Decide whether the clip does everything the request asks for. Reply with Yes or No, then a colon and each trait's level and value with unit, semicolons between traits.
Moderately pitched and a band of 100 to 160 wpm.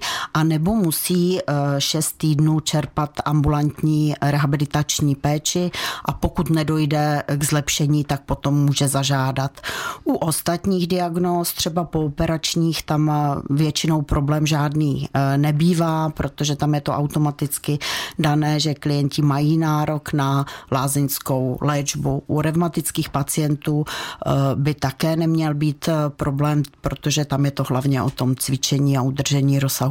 Yes: medium, 150 Hz; average, 120 wpm